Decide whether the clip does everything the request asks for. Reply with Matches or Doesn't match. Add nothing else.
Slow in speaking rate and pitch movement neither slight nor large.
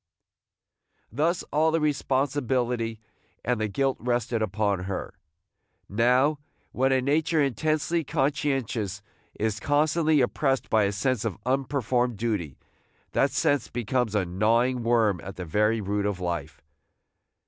Matches